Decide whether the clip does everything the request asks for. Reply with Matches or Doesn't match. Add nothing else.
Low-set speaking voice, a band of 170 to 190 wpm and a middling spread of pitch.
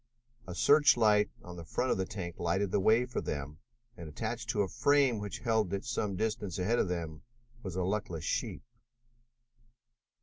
Matches